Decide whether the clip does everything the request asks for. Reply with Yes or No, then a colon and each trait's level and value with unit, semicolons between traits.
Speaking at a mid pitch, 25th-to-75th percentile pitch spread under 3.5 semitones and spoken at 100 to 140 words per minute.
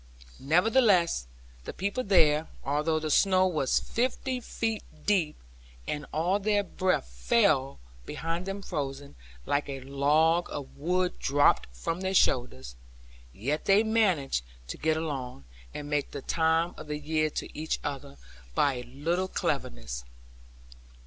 No: medium, 155 Hz; average, 5.0 semitones; slow, 135 wpm